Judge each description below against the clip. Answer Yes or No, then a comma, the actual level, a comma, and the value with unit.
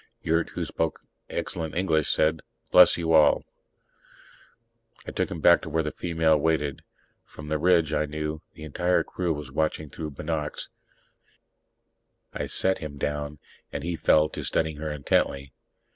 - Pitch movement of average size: No, narrow, 1.6 semitones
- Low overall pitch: Yes, very low, 80 Hz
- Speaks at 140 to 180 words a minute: Yes, average, 155 wpm